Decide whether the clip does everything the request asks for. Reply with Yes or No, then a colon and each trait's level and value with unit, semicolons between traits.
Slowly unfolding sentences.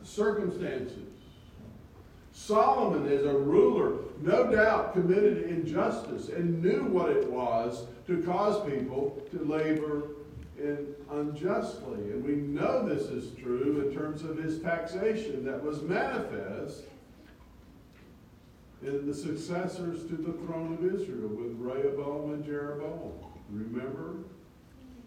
Yes: slow, 115 wpm